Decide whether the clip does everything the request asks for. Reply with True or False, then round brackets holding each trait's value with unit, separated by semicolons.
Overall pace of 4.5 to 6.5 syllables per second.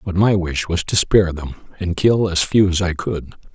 True (5.2 syllables/s)